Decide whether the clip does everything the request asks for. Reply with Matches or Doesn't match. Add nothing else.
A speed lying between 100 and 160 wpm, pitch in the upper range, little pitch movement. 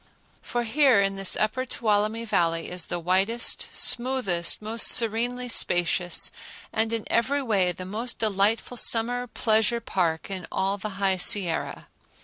Doesn't match